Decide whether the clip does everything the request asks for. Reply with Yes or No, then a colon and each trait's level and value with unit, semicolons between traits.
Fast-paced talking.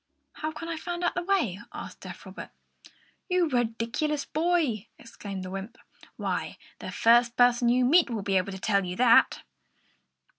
No: average, 170 wpm